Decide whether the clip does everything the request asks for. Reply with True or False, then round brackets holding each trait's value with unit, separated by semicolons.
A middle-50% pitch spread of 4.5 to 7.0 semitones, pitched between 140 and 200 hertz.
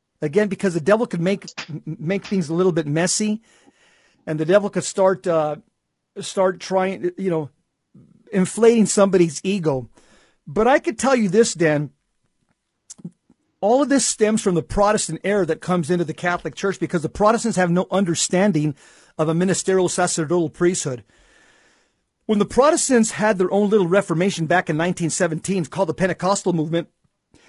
False (3.5 semitones; 185 Hz)